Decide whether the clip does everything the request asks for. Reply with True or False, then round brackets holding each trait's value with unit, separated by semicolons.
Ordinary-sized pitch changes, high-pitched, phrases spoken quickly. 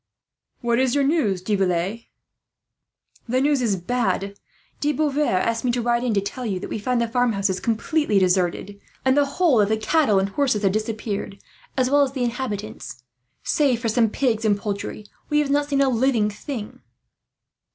False (4.7 semitones; 230 Hz; 185 wpm)